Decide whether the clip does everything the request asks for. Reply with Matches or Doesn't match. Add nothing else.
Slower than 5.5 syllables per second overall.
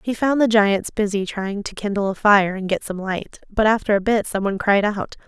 Matches